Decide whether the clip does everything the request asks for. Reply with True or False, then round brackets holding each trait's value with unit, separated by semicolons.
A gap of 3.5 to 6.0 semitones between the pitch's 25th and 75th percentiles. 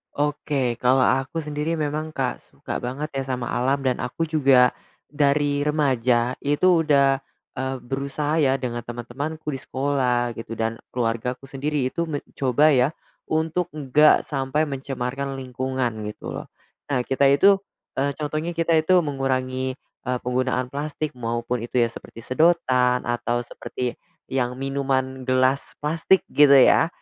False (2.9 semitones)